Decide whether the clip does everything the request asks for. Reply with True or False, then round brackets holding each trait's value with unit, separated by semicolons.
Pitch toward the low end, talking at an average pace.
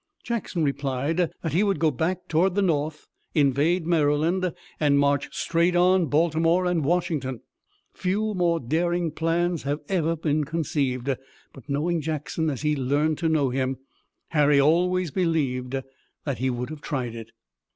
False (155 Hz; 150 wpm)